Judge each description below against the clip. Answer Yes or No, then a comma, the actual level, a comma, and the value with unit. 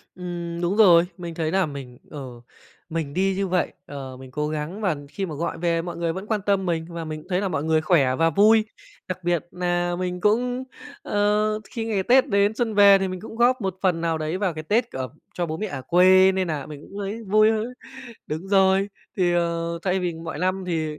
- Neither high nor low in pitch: Yes, medium, 180 Hz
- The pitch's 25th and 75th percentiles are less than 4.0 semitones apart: Yes, average, 3.5 semitones